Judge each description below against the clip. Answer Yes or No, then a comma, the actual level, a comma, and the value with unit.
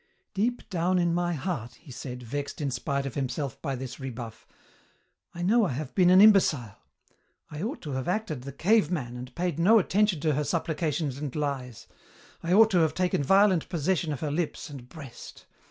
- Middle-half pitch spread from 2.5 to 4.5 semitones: No, average, 5.3 semitones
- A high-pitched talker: No, medium, 155 Hz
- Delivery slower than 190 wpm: No, average, 195 wpm